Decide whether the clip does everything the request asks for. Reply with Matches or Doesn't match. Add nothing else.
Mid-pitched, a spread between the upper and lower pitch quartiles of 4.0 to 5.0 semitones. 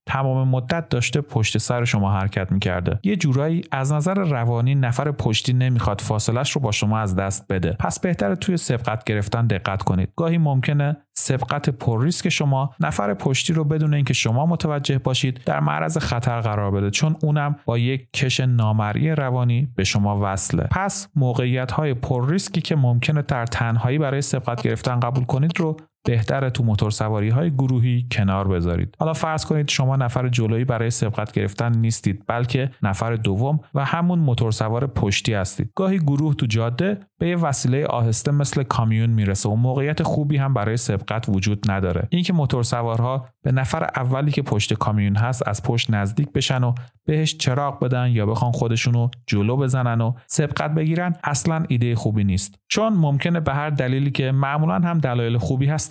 Doesn't match